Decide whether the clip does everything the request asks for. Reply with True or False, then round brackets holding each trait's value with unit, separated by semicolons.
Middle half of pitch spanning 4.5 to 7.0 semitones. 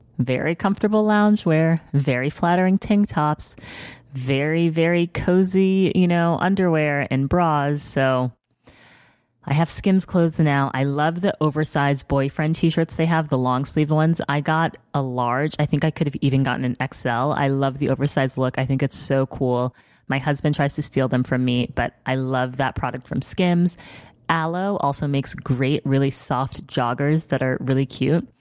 False (3.8 semitones)